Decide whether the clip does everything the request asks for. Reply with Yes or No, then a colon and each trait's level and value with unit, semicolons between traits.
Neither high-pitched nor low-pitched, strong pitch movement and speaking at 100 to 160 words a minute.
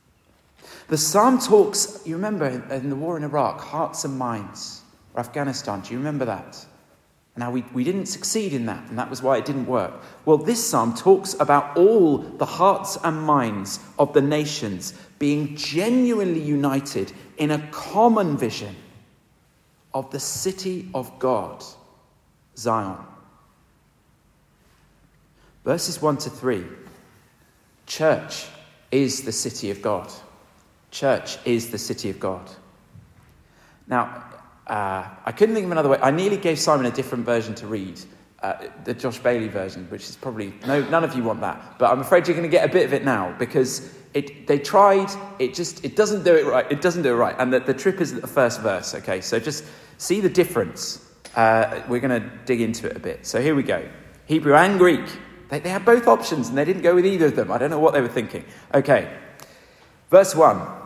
No: medium, 145 Hz; wide, 6.7 semitones; average, 185 wpm